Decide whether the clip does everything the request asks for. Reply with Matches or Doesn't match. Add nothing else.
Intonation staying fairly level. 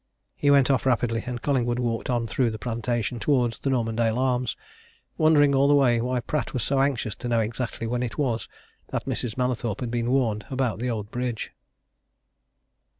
Matches